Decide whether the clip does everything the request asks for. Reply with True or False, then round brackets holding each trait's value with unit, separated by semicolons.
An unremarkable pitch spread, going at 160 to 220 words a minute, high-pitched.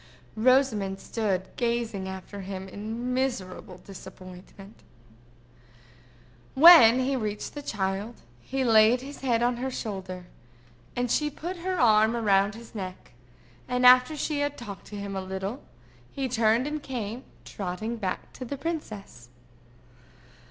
False (4.7 semitones; 140 wpm; 225 Hz)